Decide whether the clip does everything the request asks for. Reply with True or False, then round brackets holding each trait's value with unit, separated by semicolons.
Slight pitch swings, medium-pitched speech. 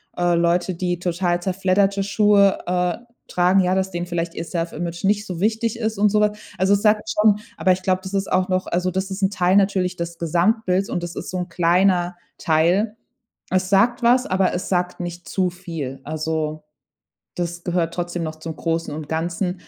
True (2.2 semitones; 180 Hz)